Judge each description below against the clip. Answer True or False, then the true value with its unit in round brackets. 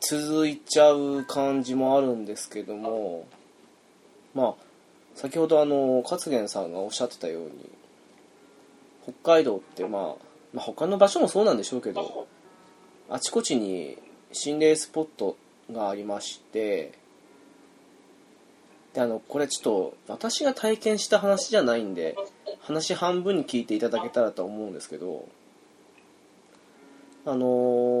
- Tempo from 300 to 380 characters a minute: False (265 characters per minute)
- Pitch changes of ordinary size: False (7.3 semitones)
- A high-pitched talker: False (145 Hz)